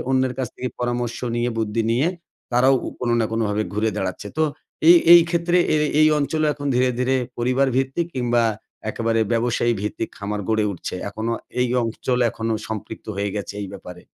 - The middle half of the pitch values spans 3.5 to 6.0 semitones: No, average, 2.9 semitones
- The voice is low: Yes, low, 120 Hz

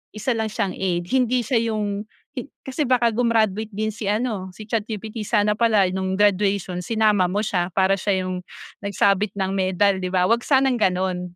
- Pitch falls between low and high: No, high, 205 Hz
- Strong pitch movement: No, average, 2.8 semitones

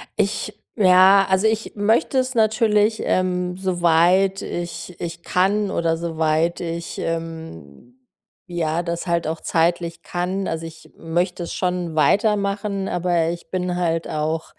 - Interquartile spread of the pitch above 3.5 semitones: No, average, 2.8 semitones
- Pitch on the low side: No, medium, 175 Hz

